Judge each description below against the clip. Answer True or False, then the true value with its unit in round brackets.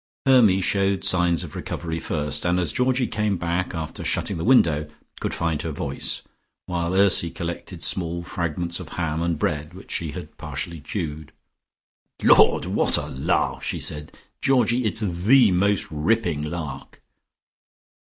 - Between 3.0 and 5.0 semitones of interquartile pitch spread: True (3.6 semitones)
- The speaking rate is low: False (150 wpm)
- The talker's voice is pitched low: True (85 Hz)